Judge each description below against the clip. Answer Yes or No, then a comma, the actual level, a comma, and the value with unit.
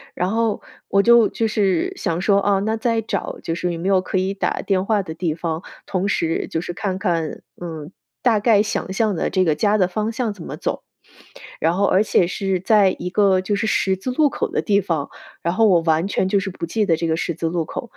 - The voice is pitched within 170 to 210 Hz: Yes, high, 190 Hz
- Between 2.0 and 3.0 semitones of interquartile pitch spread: No, average, 3.5 semitones